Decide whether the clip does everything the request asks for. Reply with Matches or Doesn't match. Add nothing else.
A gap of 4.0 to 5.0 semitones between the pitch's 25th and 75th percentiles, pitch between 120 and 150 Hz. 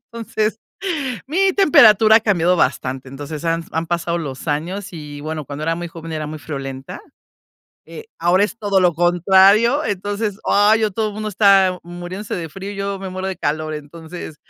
Doesn't match